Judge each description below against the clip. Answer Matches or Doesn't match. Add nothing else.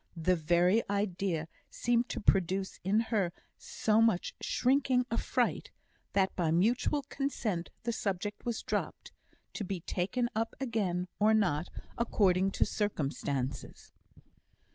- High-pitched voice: Matches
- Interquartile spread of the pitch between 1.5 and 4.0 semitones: Doesn't match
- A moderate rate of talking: Doesn't match